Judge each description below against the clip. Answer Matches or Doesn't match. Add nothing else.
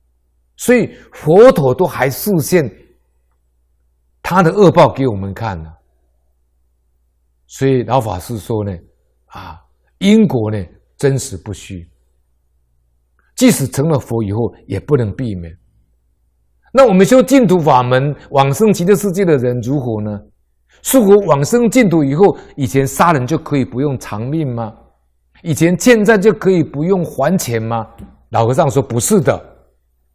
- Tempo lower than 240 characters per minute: Matches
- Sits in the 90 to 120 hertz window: Matches